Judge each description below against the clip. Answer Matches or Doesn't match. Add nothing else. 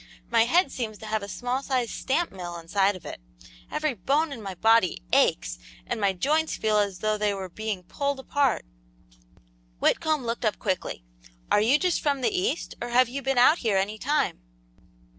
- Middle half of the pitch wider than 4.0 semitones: Matches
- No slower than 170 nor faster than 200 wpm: Matches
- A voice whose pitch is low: Doesn't match